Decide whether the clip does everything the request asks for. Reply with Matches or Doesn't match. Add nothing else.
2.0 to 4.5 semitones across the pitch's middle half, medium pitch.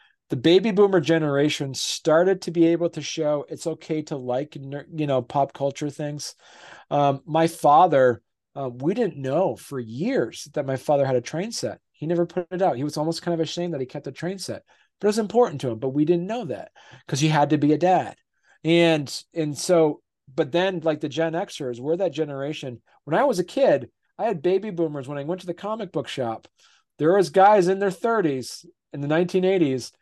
Matches